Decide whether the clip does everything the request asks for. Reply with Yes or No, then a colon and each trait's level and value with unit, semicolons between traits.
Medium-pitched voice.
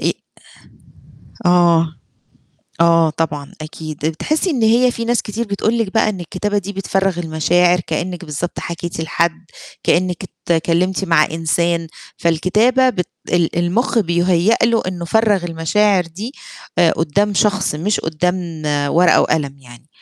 Yes: medium, 175 Hz